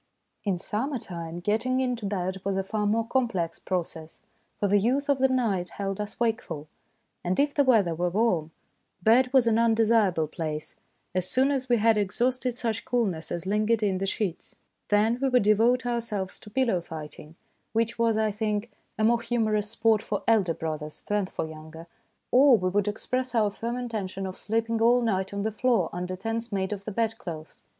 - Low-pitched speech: No, high, 215 Hz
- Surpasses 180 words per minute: Yes, average, 190 wpm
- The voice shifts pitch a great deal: No, average, 3.8 semitones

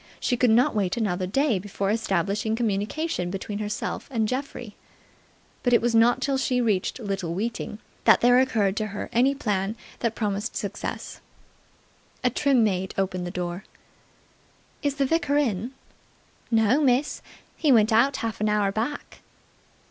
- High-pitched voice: Yes, high, 220 Hz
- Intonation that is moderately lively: Yes, average, 4.0 semitones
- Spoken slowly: No, average, 155 wpm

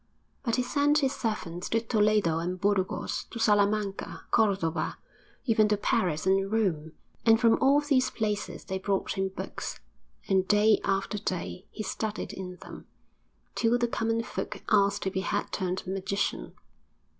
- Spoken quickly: No, average, 155 wpm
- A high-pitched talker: Yes, high, 205 Hz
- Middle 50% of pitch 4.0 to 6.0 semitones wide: No, average, 3.0 semitones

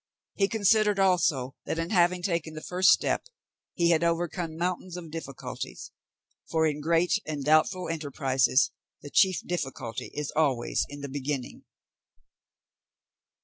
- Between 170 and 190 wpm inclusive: No, slow, 135 wpm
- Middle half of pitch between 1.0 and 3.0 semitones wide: No, average, 3.7 semitones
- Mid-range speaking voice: Yes, medium, 165 Hz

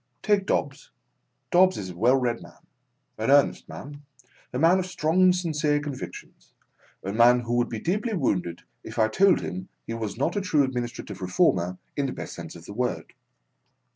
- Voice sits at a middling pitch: No, low, 130 Hz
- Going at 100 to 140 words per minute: No, average, 185 wpm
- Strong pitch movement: Yes, wide, 7.7 semitones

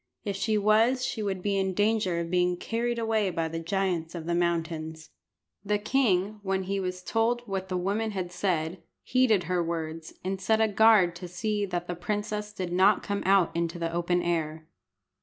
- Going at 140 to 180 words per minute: No, average, 195 wpm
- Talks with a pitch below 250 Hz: Yes, high, 190 Hz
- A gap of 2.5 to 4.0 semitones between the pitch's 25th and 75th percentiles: Yes, average, 3.4 semitones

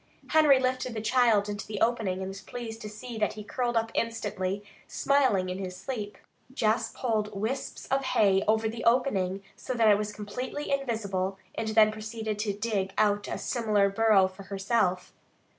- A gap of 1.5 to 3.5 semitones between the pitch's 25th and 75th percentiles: Yes, average, 2.8 semitones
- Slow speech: No, average, 175 wpm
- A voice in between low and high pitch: No, high, 215 Hz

